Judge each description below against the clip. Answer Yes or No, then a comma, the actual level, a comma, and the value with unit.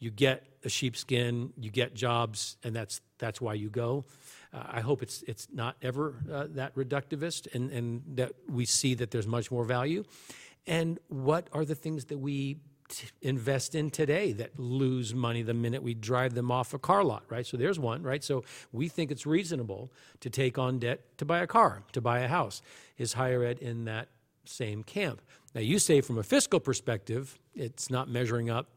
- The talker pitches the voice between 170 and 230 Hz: No, low, 130 Hz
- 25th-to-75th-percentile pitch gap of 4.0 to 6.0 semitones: No, average, 3.0 semitones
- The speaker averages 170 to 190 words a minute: No, average, 200 wpm